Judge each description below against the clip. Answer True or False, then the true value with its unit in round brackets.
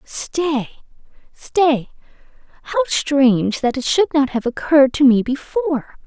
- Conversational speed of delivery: False (110 wpm)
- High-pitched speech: True (260 Hz)